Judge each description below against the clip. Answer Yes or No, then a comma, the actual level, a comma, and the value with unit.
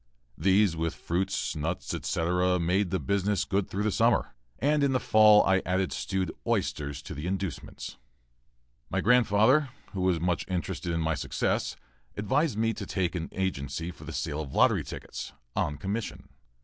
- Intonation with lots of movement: No, average, 3.8 semitones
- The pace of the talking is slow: No, average, 165 wpm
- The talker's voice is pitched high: No, very low, 95 Hz